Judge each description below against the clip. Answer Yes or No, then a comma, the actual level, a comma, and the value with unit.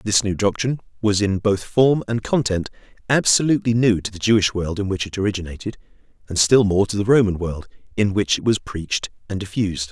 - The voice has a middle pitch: No, low, 105 Hz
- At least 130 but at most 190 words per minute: No, average, 200 wpm